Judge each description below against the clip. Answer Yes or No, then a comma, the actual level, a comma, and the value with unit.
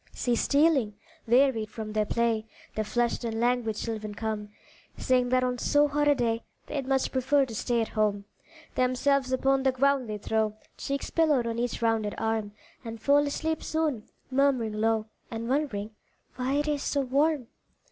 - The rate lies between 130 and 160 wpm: No, average, 170 wpm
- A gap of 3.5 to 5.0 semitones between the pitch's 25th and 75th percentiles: Yes, average, 3.9 semitones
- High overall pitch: Yes, high, 245 Hz